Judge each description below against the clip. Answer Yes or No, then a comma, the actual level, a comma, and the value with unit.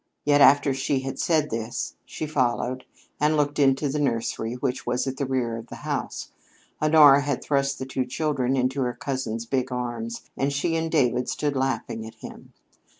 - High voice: No, low, 135 Hz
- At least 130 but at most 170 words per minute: No, average, 185 wpm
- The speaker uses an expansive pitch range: No, average, 2.7 semitones